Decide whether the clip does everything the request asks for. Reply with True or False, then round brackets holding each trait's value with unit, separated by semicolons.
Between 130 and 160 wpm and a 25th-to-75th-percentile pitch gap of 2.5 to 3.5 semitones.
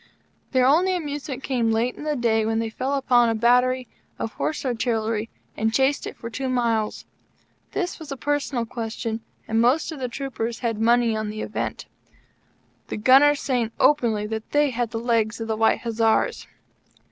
False (180 wpm; 3.1 semitones)